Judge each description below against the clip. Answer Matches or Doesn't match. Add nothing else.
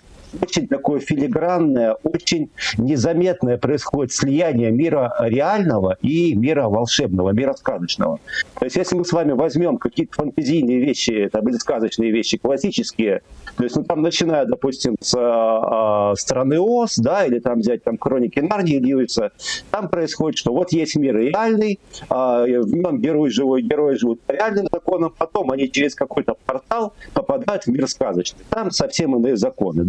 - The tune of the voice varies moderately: Doesn't match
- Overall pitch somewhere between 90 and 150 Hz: Matches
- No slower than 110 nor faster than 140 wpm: Doesn't match